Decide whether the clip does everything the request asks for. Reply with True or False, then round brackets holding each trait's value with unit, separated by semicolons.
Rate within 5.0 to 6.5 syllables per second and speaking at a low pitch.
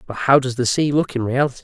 False (6.9 syllables/s; 130 Hz)